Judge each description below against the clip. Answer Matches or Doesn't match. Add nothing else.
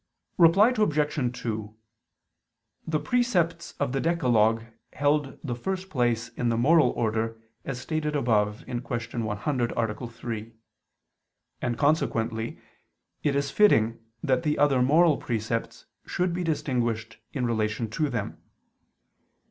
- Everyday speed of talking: Doesn't match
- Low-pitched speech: Matches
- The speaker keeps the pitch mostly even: Doesn't match